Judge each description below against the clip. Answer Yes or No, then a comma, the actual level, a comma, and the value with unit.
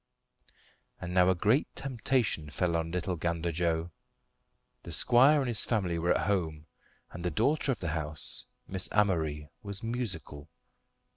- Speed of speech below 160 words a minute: Yes, average, 150 wpm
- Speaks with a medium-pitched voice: No, very low, 90 Hz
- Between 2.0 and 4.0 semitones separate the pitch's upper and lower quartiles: No, average, 5.0 semitones